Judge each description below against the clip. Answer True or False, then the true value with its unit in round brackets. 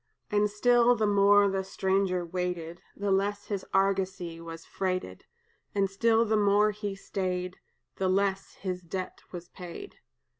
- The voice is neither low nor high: False (195 Hz)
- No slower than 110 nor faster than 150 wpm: True (145 wpm)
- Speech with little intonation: True (2.0 semitones)